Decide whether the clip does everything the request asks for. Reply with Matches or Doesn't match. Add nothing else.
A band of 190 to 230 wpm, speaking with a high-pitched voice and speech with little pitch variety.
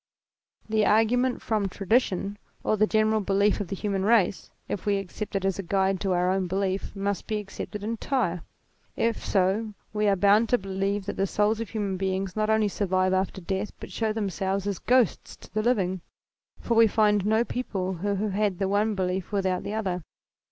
Matches